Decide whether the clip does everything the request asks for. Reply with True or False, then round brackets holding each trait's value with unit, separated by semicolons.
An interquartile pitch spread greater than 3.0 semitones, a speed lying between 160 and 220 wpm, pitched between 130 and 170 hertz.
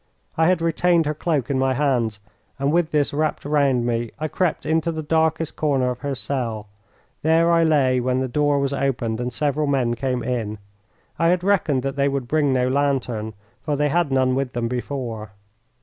True (3.6 semitones; 195 wpm; 140 Hz)